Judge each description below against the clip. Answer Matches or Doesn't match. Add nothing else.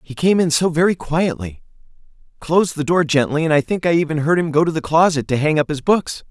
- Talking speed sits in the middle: Doesn't match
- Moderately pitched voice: Matches